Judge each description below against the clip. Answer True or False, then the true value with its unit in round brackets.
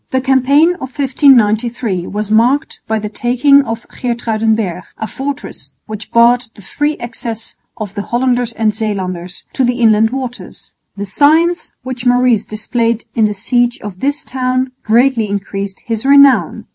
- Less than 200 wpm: True (150 wpm)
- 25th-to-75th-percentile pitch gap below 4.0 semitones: True (3.4 semitones)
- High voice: True (235 Hz)